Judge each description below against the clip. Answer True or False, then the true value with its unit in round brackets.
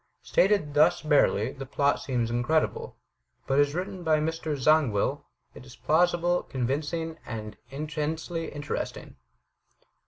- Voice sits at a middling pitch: True (150 Hz)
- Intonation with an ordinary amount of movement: True (3.2 semitones)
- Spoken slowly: True (120 wpm)